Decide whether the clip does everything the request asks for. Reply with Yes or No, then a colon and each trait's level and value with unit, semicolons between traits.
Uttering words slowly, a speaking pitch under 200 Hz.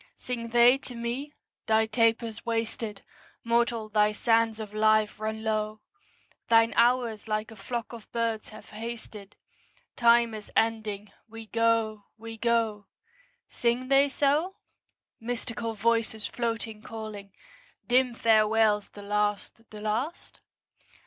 No: slow, 120 wpm; high, 225 Hz